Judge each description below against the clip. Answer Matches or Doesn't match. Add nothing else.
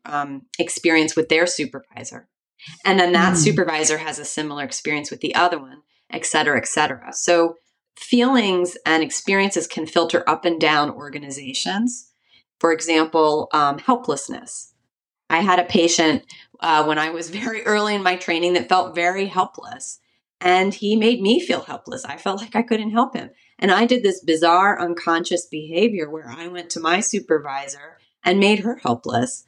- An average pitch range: Matches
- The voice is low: Doesn't match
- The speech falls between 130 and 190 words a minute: Matches